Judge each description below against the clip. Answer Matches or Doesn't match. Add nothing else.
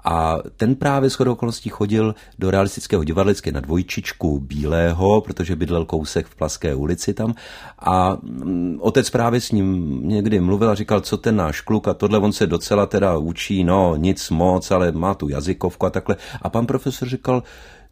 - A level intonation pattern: Doesn't match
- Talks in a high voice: Doesn't match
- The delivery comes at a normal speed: Doesn't match